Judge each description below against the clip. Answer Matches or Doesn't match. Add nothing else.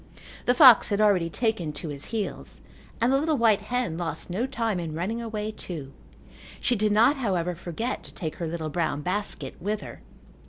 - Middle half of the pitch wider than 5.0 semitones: Matches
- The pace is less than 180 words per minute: Doesn't match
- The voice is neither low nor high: Doesn't match